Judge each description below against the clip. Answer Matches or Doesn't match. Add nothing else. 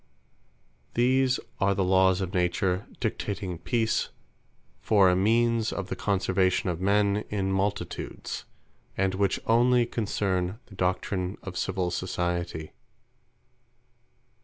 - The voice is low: Matches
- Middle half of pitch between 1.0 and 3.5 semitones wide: Matches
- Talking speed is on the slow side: Matches